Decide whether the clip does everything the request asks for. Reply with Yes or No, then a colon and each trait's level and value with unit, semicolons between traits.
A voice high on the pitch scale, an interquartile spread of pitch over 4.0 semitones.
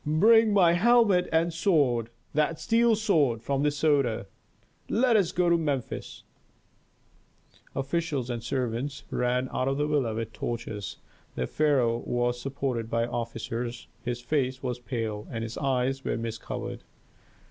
No: low, 135 Hz; wide, 5.4 semitones